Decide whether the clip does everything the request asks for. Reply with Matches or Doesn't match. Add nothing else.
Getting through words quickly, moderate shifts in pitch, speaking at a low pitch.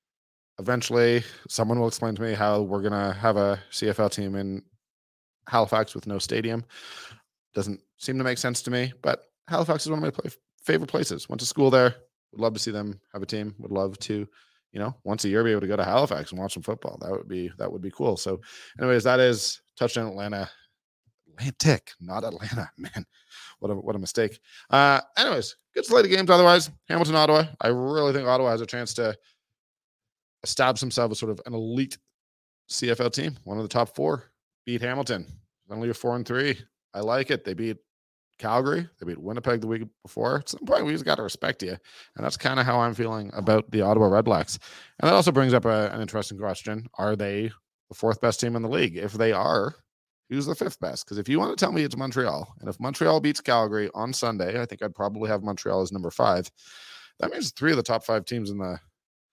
Matches